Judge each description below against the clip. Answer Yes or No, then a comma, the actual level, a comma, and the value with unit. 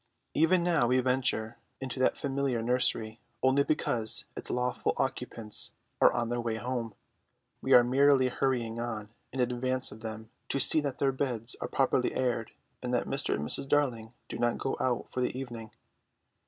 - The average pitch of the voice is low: Yes, low, 125 Hz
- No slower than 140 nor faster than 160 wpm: No, average, 175 wpm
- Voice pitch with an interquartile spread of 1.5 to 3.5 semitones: Yes, narrow, 2.5 semitones